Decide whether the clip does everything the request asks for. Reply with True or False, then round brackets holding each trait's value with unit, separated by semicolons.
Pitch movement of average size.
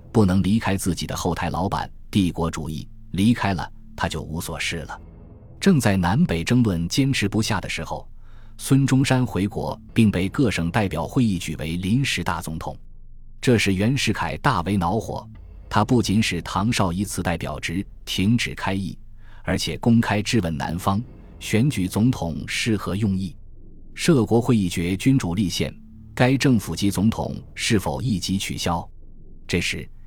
True (4.6 semitones)